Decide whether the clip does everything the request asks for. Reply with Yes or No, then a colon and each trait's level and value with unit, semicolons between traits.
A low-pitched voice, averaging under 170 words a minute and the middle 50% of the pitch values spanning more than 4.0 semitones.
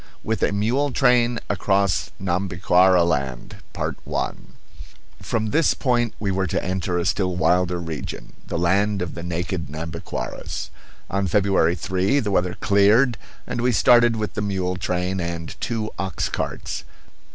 No: very low, 95 Hz; average, 140 wpm; average, 3.4 semitones